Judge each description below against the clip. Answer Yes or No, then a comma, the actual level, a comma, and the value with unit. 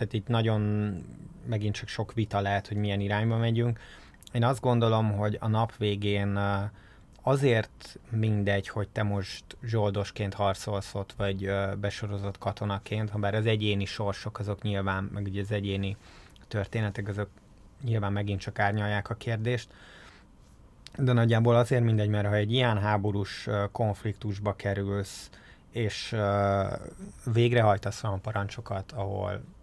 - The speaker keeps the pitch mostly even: Yes, narrow, 2.0 semitones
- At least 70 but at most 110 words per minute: No, average, 130 wpm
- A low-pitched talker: Yes, low, 105 Hz